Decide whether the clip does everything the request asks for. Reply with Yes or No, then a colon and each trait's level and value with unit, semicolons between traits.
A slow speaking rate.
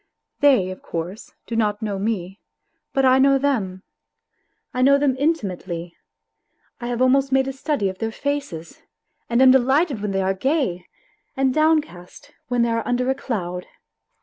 No: average, 165 wpm